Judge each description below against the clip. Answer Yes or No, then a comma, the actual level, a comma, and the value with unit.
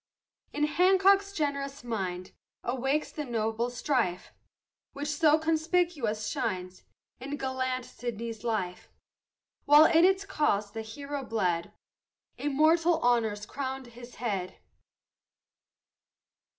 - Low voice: No, very high, 260 Hz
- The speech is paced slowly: Yes, slow, 100 wpm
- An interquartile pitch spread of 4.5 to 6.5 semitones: Yes, wide, 5.4 semitones